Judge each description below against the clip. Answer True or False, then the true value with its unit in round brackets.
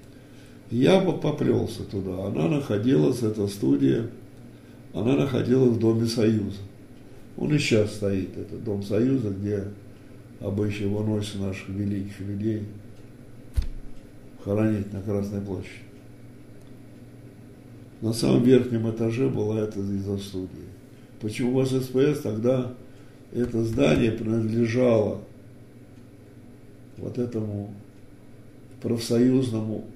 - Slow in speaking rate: True (95 wpm)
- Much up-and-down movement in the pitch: False (3.8 semitones)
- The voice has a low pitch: True (110 Hz)